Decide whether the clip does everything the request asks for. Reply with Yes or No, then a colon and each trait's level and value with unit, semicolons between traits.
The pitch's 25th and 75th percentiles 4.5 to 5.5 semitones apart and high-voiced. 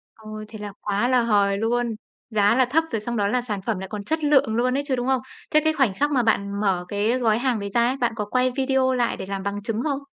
No: average, 3.8 semitones; high, 230 Hz